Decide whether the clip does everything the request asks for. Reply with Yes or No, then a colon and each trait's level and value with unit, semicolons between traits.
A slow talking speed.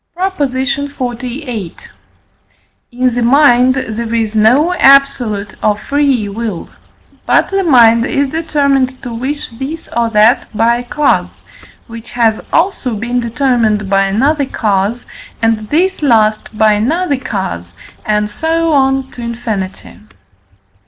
Yes: slow, 125 wpm